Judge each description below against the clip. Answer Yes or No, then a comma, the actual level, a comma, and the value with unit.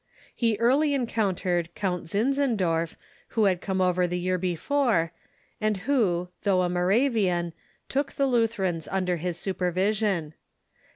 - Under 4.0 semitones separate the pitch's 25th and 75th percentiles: No, average, 4.5 semitones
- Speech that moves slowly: Yes, slow, 130 wpm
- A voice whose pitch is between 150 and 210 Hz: Yes, high, 190 Hz